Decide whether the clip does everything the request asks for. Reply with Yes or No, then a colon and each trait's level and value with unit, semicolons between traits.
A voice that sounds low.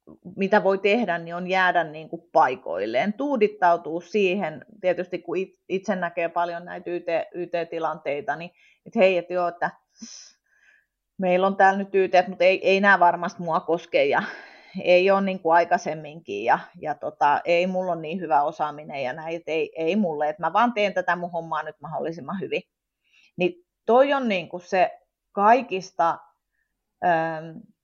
No: medium, 180 Hz